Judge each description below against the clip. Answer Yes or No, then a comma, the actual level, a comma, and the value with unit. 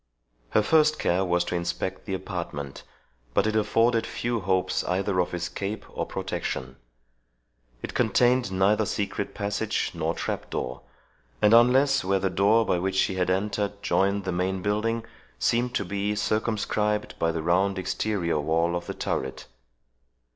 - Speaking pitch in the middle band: No, low, 100 Hz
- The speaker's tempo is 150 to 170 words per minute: Yes, average, 155 wpm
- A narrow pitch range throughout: No, average, 3.2 semitones